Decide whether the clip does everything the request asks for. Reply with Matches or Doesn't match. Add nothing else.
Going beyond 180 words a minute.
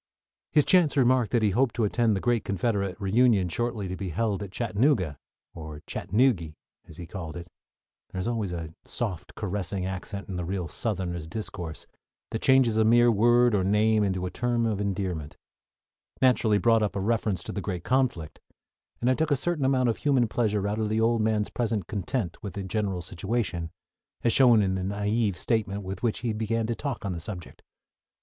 Matches